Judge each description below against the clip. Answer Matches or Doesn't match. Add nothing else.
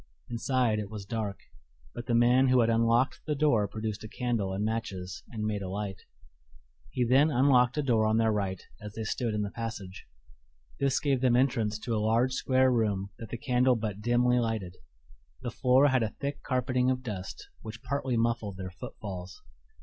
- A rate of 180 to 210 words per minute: Matches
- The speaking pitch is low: Matches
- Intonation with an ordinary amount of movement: Matches